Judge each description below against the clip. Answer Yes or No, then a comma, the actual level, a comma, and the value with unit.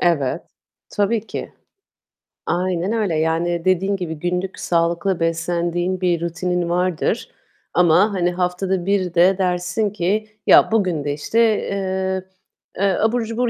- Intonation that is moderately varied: No, narrow, 2.3 semitones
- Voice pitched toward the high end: No, medium, 180 Hz